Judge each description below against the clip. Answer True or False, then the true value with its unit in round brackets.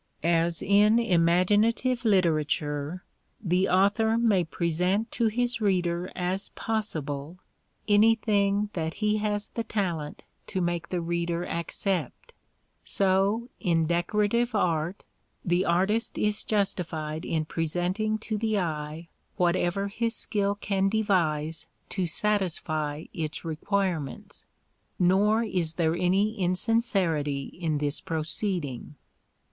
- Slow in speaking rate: True (110 wpm)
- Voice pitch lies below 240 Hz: True (185 Hz)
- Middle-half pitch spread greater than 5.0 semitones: False (4.1 semitones)